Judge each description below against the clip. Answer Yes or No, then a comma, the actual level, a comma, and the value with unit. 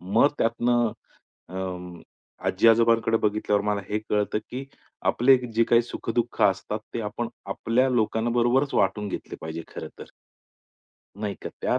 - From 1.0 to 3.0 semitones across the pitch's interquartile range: Yes, narrow, 2.5 semitones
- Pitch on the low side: Yes, low, 110 Hz